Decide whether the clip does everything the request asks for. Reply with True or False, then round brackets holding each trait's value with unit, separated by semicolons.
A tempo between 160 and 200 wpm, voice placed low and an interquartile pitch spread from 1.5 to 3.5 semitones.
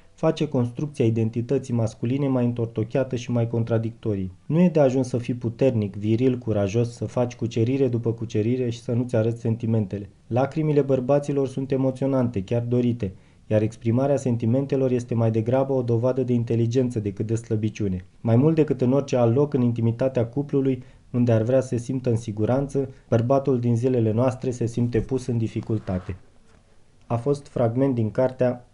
True (165 wpm; 120 Hz; 2.8 semitones)